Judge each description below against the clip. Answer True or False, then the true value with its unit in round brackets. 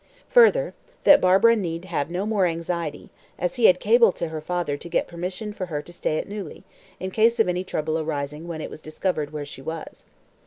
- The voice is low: False (175 Hz)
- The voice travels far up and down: False (4.3 semitones)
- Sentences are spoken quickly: True (210 wpm)